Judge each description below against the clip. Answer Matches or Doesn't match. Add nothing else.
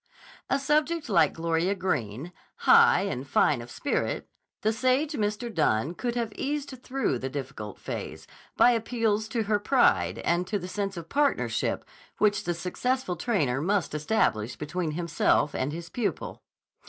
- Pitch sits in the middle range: Doesn't match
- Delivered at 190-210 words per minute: Doesn't match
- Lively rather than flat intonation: Matches